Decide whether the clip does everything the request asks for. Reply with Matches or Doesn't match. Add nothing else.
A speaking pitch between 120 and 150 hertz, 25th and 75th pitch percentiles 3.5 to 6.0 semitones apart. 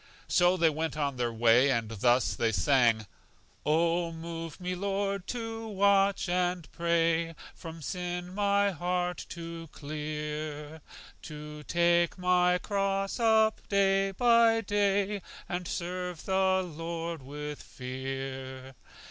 Doesn't match